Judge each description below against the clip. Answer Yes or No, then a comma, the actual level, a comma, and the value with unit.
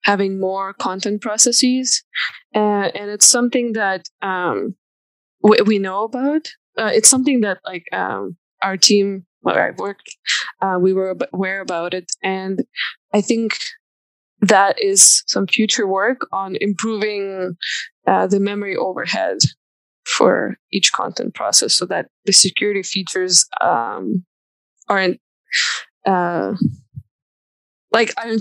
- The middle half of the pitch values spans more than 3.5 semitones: No, average, 2.8 semitones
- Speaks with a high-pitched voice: Yes, high, 200 Hz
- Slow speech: Yes, slow, 125 wpm